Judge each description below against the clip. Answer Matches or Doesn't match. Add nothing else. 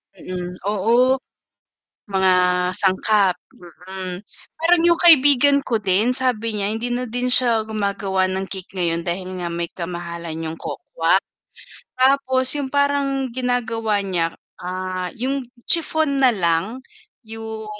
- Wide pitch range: Matches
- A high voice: Matches